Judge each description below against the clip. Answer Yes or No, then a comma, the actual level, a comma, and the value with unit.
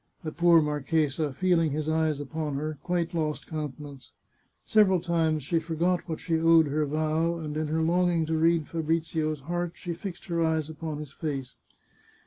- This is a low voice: No, medium, 160 Hz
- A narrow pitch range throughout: Yes, narrow, 1.8 semitones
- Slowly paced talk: No, average, 170 wpm